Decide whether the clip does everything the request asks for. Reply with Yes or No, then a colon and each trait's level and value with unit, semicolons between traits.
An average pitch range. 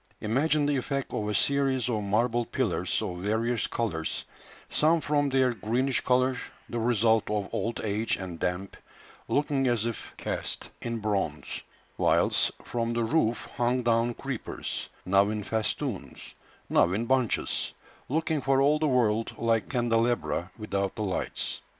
Yes: average, 3.6 semitones